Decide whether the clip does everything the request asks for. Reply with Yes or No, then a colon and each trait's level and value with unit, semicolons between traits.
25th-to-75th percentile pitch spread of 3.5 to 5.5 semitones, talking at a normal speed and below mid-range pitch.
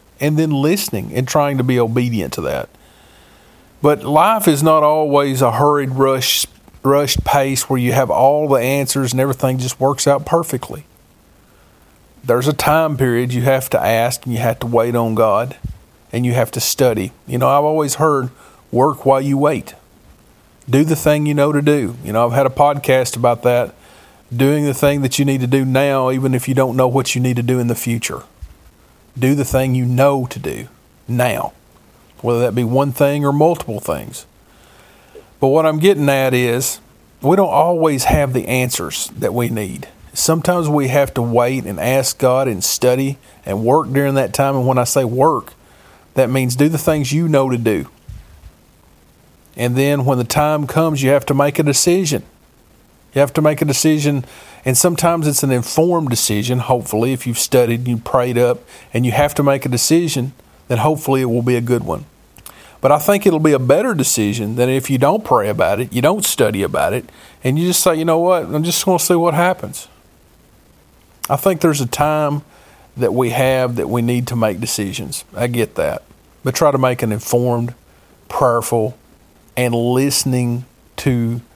No: average, 3.1 semitones; average, 195 wpm; low, 130 Hz